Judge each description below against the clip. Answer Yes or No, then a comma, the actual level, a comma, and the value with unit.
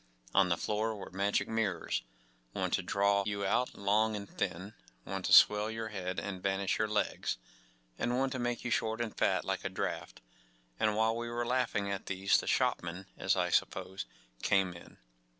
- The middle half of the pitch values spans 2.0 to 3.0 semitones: Yes, narrow, 2.5 semitones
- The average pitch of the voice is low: Yes, low, 100 Hz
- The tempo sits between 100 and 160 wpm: No, average, 185 wpm